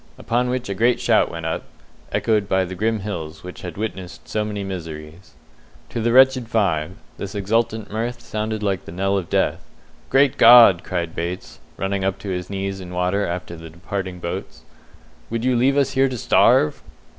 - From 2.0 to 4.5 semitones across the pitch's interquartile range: Yes, average, 4.2 semitones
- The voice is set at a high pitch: No, low, 100 Hz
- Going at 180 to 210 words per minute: Yes, average, 185 wpm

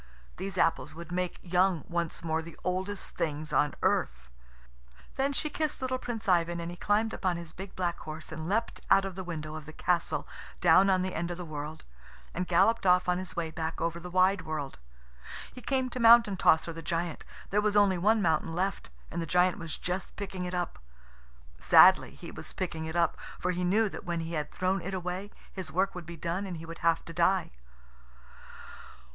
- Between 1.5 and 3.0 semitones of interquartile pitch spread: Yes, narrow, 2.6 semitones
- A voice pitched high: No, medium, 180 Hz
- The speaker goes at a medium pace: No, fast, 210 wpm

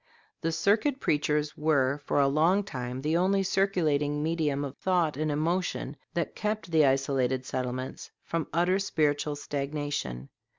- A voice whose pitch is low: No, medium, 150 Hz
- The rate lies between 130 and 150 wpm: Yes, average, 140 wpm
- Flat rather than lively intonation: No, average, 3.7 semitones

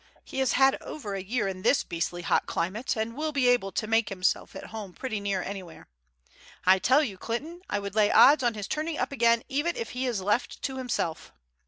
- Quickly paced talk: Yes, fast, 220 wpm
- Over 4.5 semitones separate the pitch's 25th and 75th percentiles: Yes, average, 5.3 semitones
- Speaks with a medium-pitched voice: No, high, 225 Hz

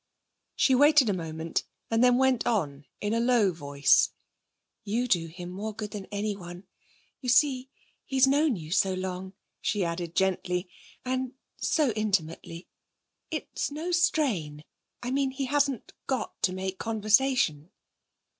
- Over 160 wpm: No, average, 140 wpm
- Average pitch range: No, wide, 6.4 semitones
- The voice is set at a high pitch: Yes, high, 210 Hz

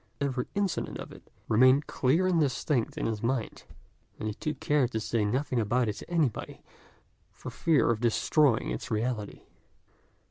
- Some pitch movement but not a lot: Yes, average, 4.8 semitones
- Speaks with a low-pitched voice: Yes, low, 125 Hz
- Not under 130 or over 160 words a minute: No, average, 170 wpm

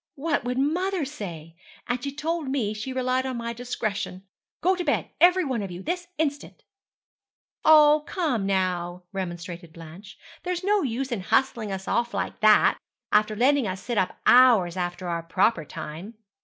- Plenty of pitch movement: Yes, wide, 7.3 semitones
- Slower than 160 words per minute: No, average, 170 wpm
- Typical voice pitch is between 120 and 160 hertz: No, high, 235 Hz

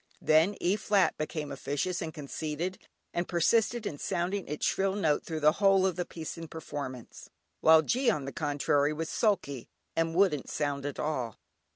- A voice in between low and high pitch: Yes, medium, 160 Hz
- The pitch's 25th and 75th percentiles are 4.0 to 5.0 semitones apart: Yes, average, 4.3 semitones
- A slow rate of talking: No, average, 175 wpm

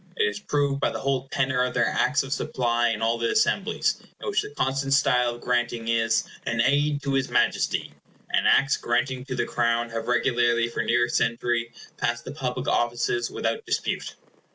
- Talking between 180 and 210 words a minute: Yes, average, 195 wpm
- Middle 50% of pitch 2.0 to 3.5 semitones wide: Yes, narrow, 2.5 semitones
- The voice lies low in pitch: Yes, low, 120 Hz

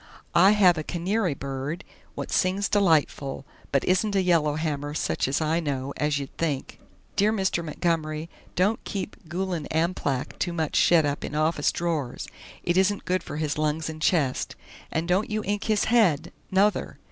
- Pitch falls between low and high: Yes, medium, 165 Hz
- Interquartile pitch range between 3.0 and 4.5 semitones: Yes, average, 4.0 semitones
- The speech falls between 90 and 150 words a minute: No, average, 170 wpm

